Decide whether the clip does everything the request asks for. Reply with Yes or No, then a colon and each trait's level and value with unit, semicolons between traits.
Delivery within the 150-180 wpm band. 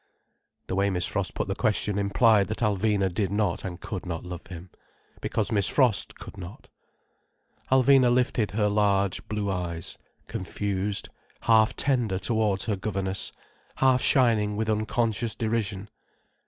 No: average, 140 wpm